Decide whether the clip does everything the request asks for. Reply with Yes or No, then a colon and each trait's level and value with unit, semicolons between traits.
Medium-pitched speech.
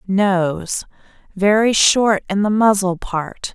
No: high, 200 Hz